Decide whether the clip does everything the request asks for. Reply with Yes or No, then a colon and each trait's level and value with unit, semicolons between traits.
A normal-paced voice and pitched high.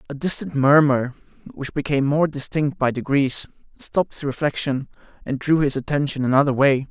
No: average, 155 wpm; medium, 140 Hz